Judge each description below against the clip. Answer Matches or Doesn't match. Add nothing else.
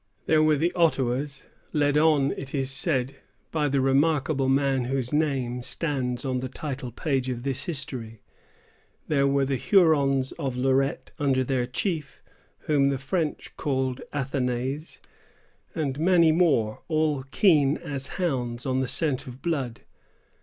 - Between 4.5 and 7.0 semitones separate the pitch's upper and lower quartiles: Doesn't match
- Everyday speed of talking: Matches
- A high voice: Doesn't match